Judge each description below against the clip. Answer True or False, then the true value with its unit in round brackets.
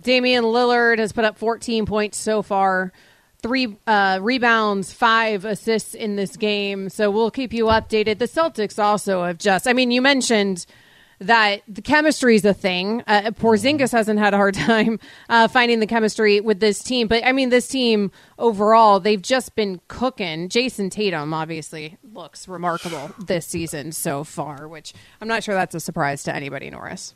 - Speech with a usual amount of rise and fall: True (3.3 semitones)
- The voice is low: False (215 Hz)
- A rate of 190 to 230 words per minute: False (175 wpm)